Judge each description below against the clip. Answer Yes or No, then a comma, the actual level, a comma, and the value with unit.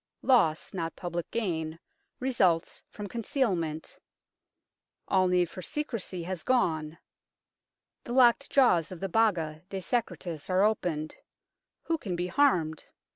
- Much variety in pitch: Yes, wide, 6.1 semitones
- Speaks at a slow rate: Yes, slow, 125 wpm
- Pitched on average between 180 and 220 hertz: Yes, medium, 185 Hz